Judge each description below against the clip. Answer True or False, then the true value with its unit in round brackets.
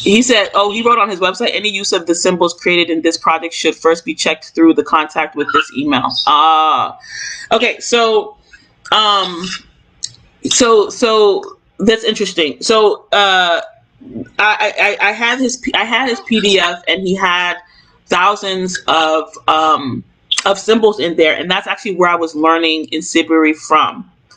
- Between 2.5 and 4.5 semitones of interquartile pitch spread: False (5.2 semitones)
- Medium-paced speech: True (165 wpm)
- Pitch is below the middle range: False (190 Hz)